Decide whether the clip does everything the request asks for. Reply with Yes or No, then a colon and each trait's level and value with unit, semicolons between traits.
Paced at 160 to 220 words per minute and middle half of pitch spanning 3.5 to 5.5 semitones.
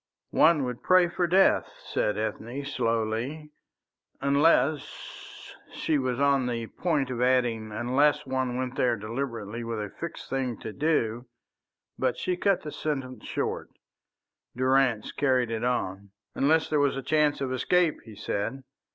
No: average, 150 wpm; average, 4.0 semitones